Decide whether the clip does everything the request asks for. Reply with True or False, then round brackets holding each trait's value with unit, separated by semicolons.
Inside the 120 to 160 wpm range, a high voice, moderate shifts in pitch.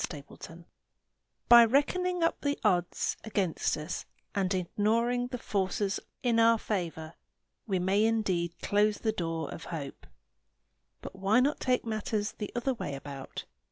True (145 wpm; 205 Hz; 4.9 semitones)